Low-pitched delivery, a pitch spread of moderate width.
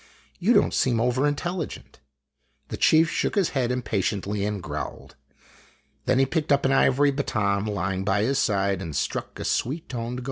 No: low, 125 Hz; wide, 5.8 semitones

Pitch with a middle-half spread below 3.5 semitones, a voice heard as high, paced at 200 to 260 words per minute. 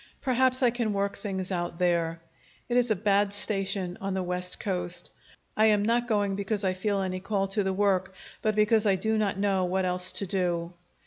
Yes: narrow, 2.5 semitones; high, 195 Hz; fast, 205 wpm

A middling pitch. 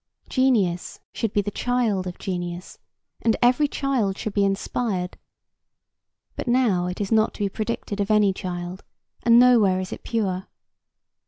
No: high, 205 Hz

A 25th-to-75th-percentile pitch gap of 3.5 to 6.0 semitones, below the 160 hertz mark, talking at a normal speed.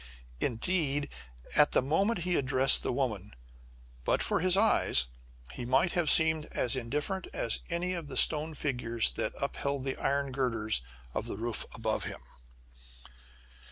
Yes: average, 5.1 semitones; medium, 140 Hz; average, 150 wpm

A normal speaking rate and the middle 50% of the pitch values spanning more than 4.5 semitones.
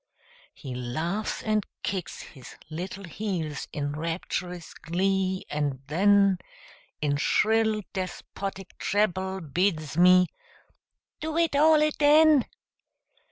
No: slow, 100 wpm; average, 4.9 semitones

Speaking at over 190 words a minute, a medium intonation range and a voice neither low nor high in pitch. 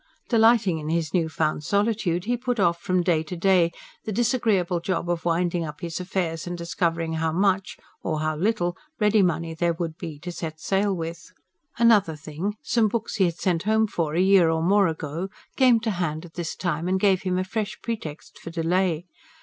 Yes: average, 200 wpm; average, 3.5 semitones; medium, 175 Hz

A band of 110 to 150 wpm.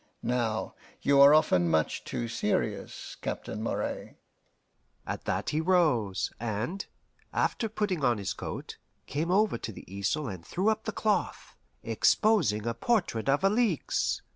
Yes: average, 140 wpm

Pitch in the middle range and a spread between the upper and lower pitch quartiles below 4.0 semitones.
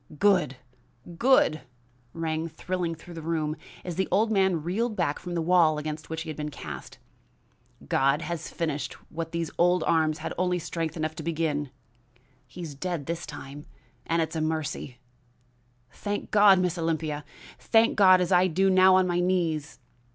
Yes: medium, 165 Hz; average, 2.7 semitones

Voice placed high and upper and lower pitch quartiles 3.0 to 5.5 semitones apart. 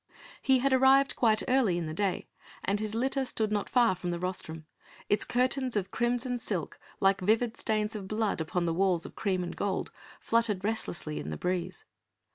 Yes: high, 210 Hz; average, 4.8 semitones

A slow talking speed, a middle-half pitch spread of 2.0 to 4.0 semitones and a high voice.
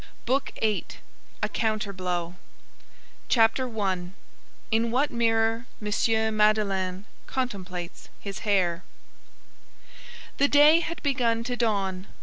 Yes: slow, 95 wpm; average, 3.7 semitones; high, 220 Hz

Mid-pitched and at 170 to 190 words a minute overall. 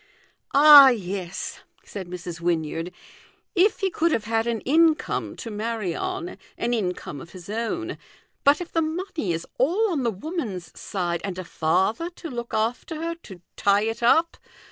No: high, 230 Hz; average, 175 wpm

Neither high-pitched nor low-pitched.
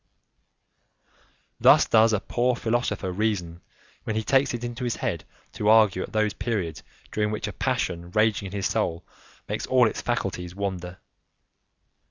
No: low, 105 Hz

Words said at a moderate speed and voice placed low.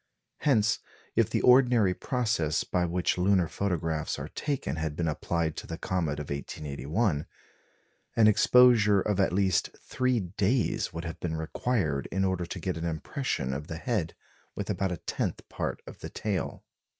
Yes: average, 165 wpm; very low, 90 Hz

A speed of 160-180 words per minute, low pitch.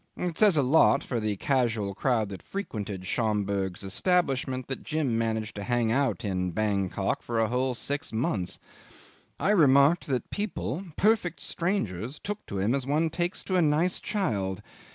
Yes: average, 165 wpm; low, 125 Hz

